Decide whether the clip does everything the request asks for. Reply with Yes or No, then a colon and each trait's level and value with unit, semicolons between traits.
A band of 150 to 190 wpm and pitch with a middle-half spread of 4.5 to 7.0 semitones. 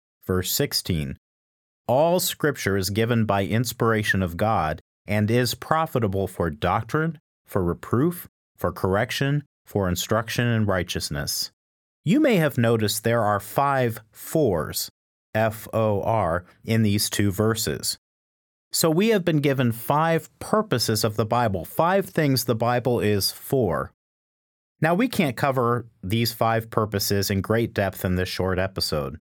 No: average, 140 wpm; average, 4.9 semitones